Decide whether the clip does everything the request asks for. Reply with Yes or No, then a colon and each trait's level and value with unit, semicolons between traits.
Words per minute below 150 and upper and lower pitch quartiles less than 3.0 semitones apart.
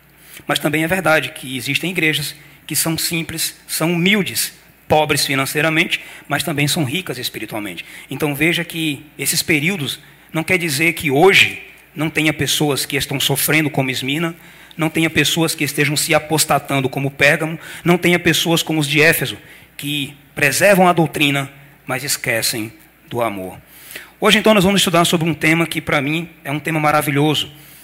No: average, 165 wpm; narrow, 2.4 semitones